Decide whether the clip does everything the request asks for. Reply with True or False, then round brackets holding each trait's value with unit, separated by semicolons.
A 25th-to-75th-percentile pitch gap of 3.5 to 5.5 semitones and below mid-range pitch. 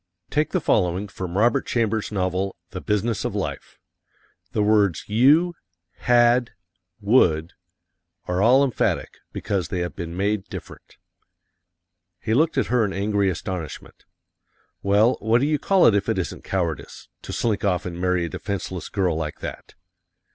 True (4.4 semitones; 100 Hz)